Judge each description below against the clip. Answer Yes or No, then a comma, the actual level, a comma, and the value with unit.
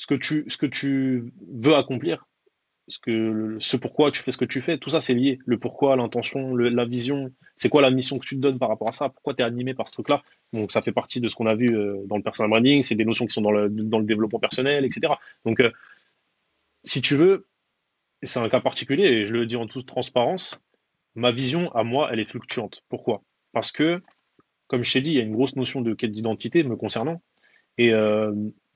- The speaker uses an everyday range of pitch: Yes, average, 3.5 semitones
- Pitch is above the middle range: No, low, 125 Hz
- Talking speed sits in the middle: No, fast, 240 wpm